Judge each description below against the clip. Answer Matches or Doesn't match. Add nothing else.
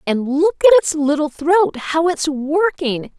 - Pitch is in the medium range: Doesn't match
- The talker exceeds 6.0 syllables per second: Doesn't match